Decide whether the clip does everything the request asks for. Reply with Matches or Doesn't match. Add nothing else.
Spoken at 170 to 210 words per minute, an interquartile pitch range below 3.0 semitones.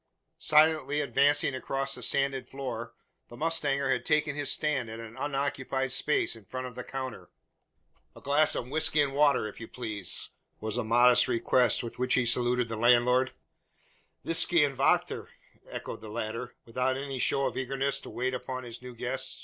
Matches